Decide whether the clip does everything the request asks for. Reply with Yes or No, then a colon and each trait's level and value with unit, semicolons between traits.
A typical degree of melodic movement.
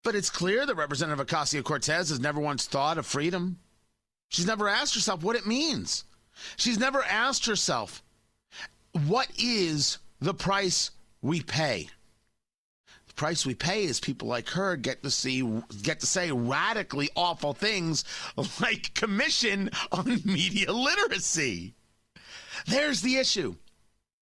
No: wide, 6.3 semitones